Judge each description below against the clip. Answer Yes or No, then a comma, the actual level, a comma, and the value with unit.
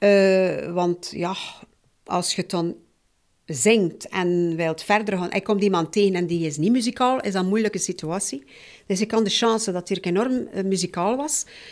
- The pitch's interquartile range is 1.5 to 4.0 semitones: Yes, average, 3.0 semitones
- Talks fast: No, average, 180 wpm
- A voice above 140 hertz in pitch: Yes, high, 190 Hz